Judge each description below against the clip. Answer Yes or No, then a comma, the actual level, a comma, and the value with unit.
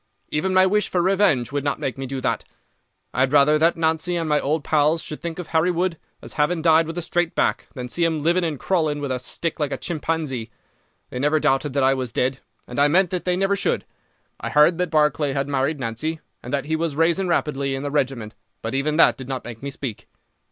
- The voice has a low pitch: No, medium, 150 Hz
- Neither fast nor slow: No, fast, 240 wpm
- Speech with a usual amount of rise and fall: Yes, average, 3.6 semitones